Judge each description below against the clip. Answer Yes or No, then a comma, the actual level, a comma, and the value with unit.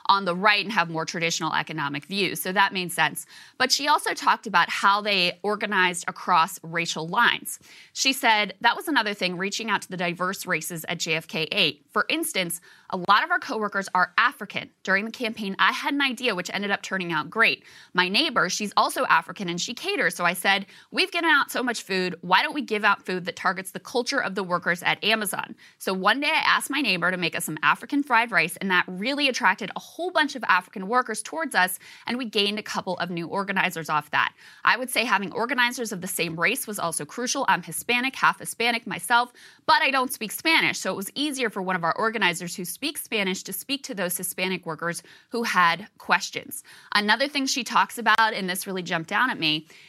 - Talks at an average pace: No, fast, 225 wpm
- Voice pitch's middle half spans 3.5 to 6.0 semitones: Yes, average, 5.1 semitones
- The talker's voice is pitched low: No, high, 200 Hz